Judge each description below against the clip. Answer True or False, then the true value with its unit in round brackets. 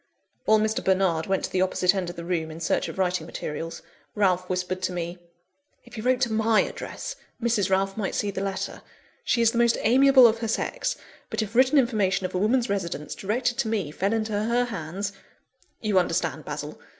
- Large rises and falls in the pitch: False (3.8 semitones)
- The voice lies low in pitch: False (200 Hz)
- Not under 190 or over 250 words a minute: True (205 wpm)